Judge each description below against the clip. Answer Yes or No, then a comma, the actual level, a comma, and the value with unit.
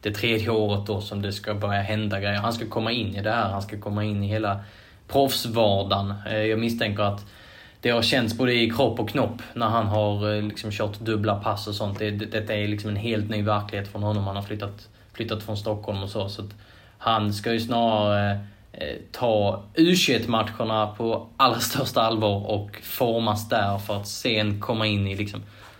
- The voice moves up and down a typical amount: No, narrow, 1.5 semitones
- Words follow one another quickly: Yes, fast, 200 wpm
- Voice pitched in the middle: No, low, 105 Hz